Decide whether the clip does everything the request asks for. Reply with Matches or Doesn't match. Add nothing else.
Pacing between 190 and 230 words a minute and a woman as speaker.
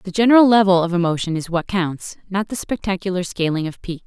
Matches